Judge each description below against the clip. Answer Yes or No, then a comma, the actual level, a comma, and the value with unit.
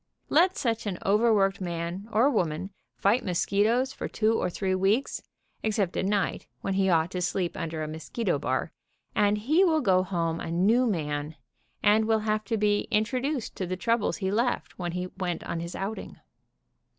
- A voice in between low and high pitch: No, high, 195 Hz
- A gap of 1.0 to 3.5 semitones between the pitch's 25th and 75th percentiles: No, average, 4.1 semitones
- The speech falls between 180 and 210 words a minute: Yes, average, 185 wpm